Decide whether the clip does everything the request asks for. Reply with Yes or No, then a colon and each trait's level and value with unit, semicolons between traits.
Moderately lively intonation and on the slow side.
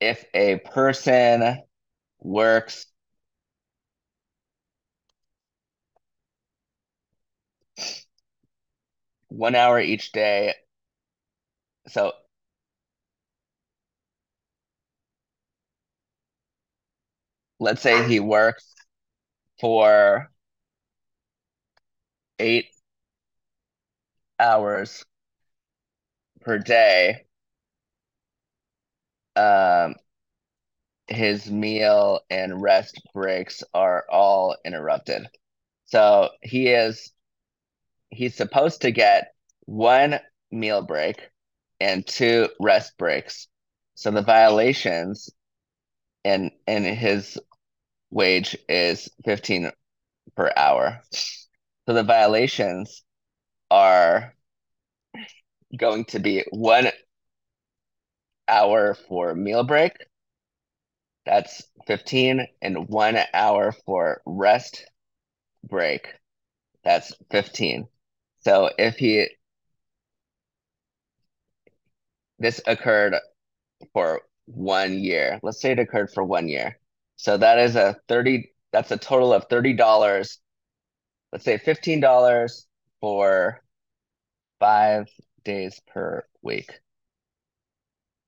Yes: average, 3.6 semitones; slow, 75 wpm